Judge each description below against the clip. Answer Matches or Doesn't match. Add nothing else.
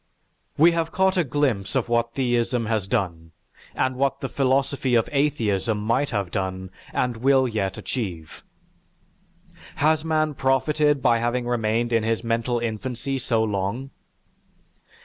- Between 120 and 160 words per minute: Matches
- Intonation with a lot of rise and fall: Doesn't match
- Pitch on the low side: Matches